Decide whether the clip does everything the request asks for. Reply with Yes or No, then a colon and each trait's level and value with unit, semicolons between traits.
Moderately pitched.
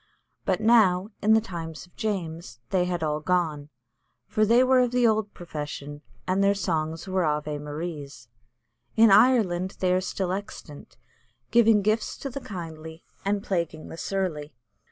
Yes: medium, 180 Hz